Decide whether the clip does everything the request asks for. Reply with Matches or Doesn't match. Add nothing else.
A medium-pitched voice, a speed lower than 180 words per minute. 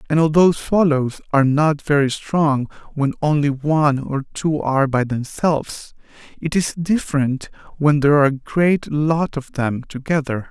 Matches